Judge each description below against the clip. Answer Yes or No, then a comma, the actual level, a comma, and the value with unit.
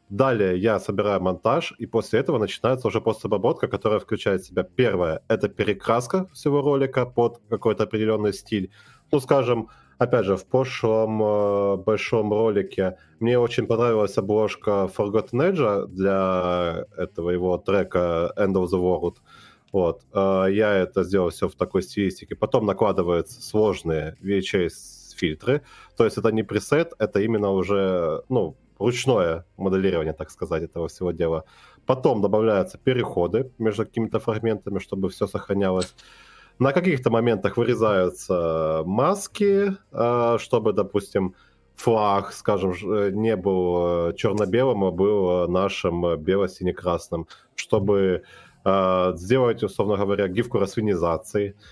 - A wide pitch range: No, average, 3.8 semitones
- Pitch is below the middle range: Yes, low, 100 Hz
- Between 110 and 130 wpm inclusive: Yes, average, 125 wpm